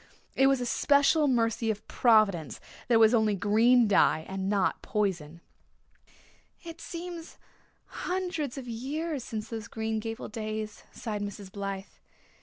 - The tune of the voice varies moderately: Yes, average, 4.6 semitones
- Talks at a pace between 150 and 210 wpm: No, average, 140 wpm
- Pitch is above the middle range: Yes, high, 225 Hz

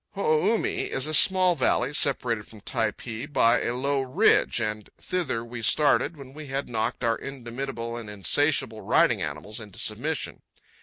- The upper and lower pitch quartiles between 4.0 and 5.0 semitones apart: Yes, average, 4.3 semitones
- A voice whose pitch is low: Yes, low, 125 Hz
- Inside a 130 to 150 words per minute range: No, average, 170 wpm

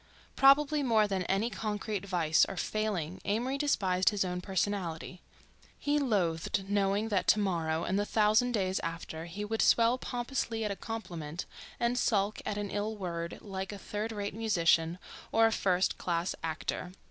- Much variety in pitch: No, average, 3.7 semitones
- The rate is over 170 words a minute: No, average, 160 wpm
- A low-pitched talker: No, high, 200 Hz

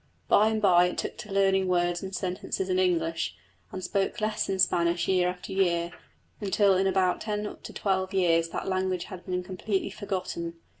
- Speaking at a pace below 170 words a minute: No, average, 185 wpm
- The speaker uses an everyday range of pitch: No, narrow, 1.6 semitones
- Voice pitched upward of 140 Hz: Yes, medium, 185 Hz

